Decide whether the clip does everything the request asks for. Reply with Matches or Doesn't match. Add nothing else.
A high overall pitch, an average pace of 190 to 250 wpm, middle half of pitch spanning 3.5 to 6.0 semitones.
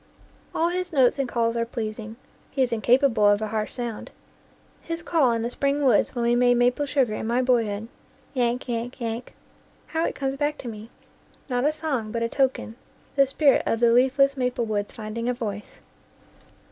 Doesn't match